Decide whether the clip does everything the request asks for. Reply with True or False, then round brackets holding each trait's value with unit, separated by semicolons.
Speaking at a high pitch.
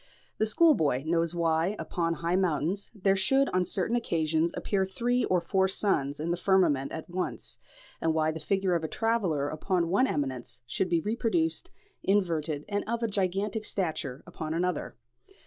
False (180 Hz)